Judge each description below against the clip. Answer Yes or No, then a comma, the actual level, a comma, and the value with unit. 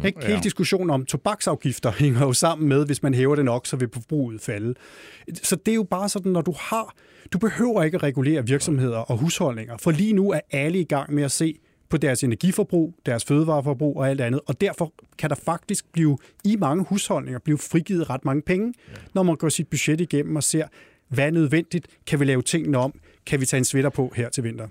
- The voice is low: No, medium, 155 Hz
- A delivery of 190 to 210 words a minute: No, average, 220 wpm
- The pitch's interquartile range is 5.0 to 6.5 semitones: No, average, 4.6 semitones